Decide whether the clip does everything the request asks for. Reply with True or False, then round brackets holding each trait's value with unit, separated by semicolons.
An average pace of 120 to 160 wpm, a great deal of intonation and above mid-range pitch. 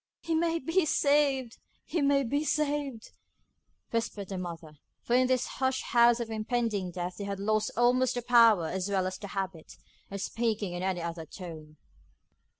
False (170 wpm; 5.7 semitones; 225 Hz)